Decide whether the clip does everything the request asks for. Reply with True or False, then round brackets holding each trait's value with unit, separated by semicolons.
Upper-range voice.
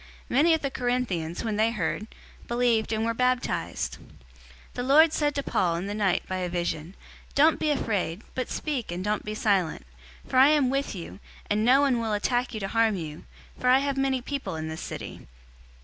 True (230 Hz)